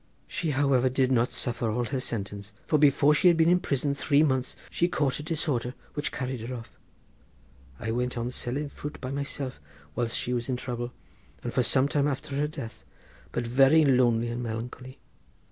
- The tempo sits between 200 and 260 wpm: No, average, 190 wpm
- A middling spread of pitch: Yes, average, 3.0 semitones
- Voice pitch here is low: Yes, low, 130 Hz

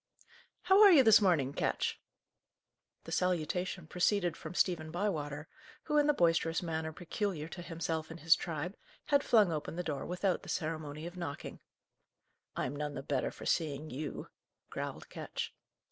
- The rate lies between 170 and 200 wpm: No, average, 160 wpm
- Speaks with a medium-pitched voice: Yes, medium, 165 Hz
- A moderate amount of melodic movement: Yes, average, 3.0 semitones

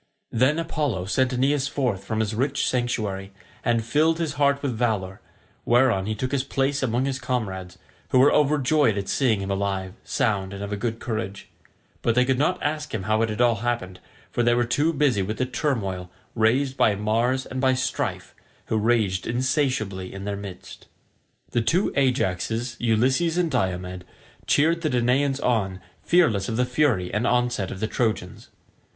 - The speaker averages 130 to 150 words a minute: No, average, 180 wpm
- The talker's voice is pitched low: Yes, low, 120 Hz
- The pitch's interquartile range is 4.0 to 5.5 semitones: Yes, average, 4.8 semitones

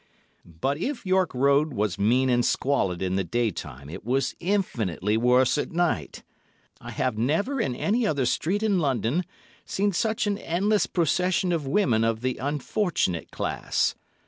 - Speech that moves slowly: No, average, 160 wpm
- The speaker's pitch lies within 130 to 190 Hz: Yes, medium, 140 Hz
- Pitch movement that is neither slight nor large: No, wide, 8.4 semitones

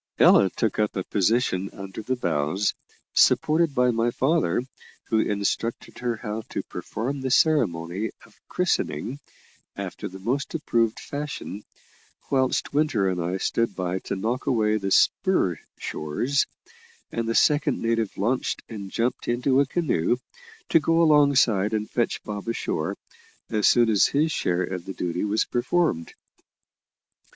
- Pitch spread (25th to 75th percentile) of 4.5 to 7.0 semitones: Yes, wide, 5.4 semitones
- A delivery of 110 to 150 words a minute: Yes, average, 145 wpm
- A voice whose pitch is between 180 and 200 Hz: No, low, 115 Hz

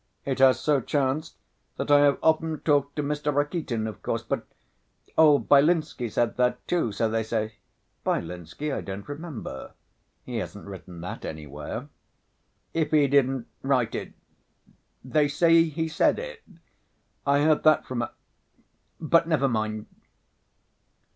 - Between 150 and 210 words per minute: No, average, 140 wpm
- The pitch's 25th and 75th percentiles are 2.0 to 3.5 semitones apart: No, average, 5.3 semitones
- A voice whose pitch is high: No, medium, 140 Hz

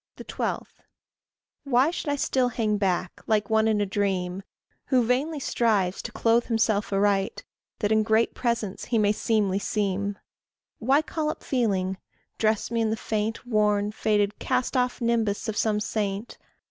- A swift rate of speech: No, average, 160 wpm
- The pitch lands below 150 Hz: No, high, 215 Hz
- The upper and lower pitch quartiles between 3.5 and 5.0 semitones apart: No, narrow, 2.5 semitones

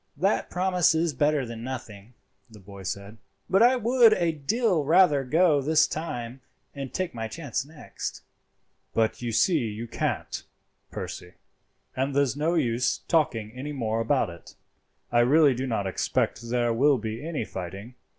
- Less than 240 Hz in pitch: Yes, low, 135 Hz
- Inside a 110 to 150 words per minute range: No, average, 160 wpm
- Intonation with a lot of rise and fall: Yes, wide, 5.9 semitones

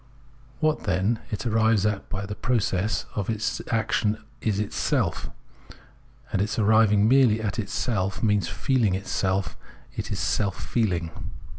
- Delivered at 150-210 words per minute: No, average, 140 wpm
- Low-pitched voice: Yes, low, 105 Hz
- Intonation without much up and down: Yes, narrow, 2.3 semitones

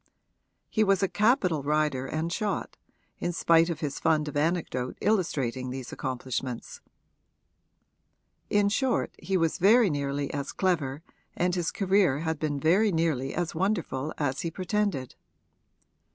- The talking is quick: No, average, 140 wpm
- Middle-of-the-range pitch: Yes, medium, 160 Hz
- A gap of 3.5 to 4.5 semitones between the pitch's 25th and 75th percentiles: No, average, 5.2 semitones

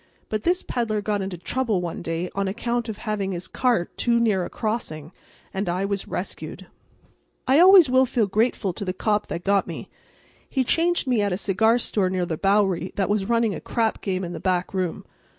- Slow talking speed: No, fast, 205 wpm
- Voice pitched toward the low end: No, high, 205 Hz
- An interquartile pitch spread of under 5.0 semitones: Yes, average, 4.0 semitones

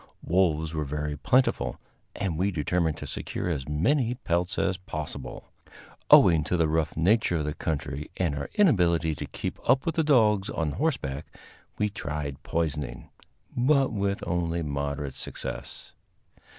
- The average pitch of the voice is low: Yes, very low, 85 Hz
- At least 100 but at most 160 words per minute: Yes, average, 150 wpm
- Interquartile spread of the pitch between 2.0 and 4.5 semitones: No, average, 5.1 semitones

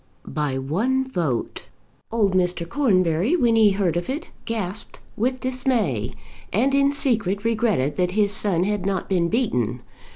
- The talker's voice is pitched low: No, high, 200 Hz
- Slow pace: No, average, 150 wpm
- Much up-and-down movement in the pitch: Yes, wide, 5.7 semitones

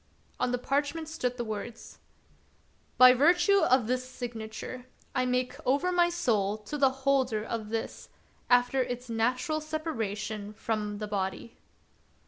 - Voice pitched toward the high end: Yes, very high, 250 Hz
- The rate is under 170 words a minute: Yes, average, 150 wpm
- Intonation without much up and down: No, average, 3.9 semitones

